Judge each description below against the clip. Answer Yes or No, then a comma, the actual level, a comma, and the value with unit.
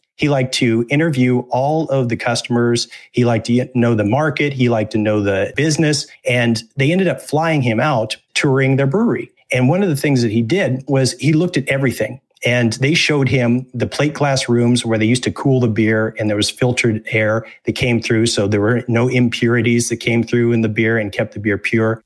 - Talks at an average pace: No, fast, 225 wpm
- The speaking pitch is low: Yes, low, 120 Hz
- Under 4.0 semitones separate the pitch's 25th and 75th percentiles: Yes, average, 3.0 semitones